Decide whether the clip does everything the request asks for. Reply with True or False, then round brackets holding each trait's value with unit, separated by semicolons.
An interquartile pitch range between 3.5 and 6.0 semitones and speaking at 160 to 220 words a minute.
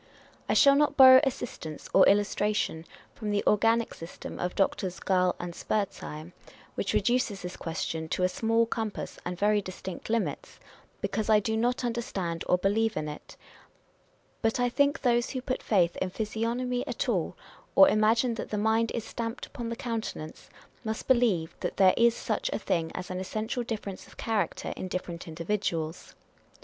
True (4.3 semitones; 170 wpm)